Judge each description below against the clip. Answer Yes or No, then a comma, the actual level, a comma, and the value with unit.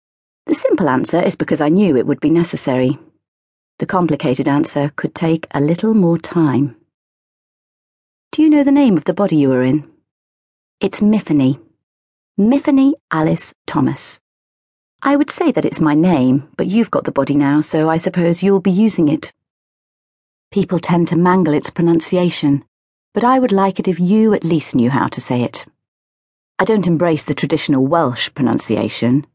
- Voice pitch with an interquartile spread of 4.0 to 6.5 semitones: Yes, wide, 5.5 semitones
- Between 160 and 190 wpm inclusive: Yes, average, 170 wpm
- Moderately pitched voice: Yes, medium, 165 Hz